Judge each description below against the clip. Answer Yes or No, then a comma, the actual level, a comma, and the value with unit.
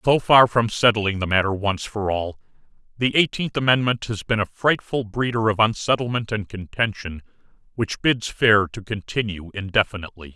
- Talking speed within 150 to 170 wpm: Yes, average, 155 wpm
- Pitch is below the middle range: Yes, low, 110 Hz